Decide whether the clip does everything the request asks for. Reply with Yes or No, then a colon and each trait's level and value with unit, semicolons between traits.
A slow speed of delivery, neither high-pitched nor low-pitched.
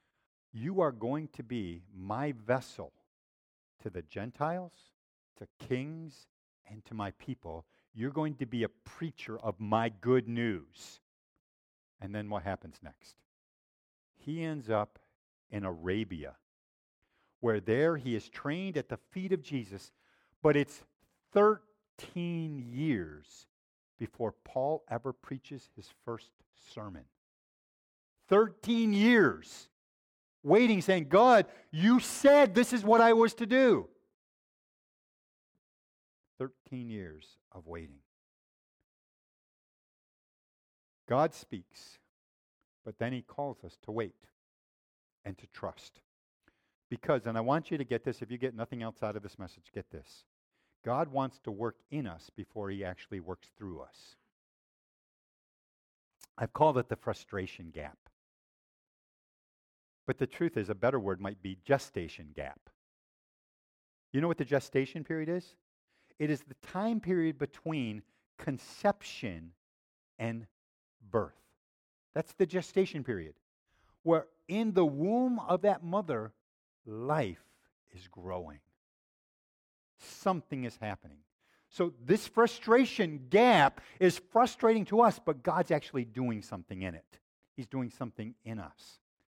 No: slow, 125 wpm; low, 125 Hz